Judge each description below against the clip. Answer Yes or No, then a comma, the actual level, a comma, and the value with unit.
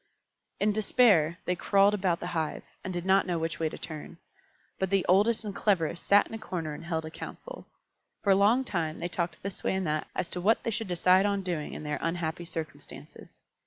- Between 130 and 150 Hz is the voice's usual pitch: No, medium, 180 Hz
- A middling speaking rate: No, fast, 220 wpm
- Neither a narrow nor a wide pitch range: Yes, average, 3.4 semitones